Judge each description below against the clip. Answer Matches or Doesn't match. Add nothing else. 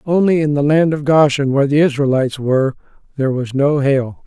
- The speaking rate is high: Doesn't match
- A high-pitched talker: Doesn't match